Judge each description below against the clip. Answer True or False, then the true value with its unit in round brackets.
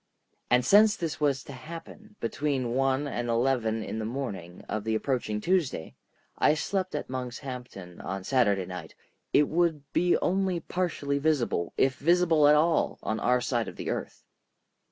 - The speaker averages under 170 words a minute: True (155 wpm)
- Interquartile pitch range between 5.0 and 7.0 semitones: True (5.5 semitones)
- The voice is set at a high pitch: False (135 Hz)